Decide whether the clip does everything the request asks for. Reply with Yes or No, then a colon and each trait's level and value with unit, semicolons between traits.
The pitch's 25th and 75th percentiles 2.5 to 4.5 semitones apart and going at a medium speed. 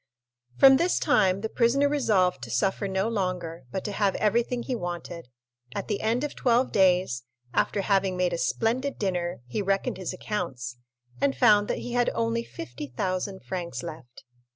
No: average, 4.9 semitones; average, 170 wpm